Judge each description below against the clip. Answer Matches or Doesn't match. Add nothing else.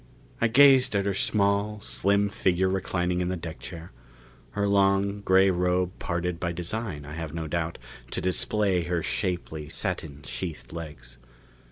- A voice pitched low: Matches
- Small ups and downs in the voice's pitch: Doesn't match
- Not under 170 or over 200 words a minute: Doesn't match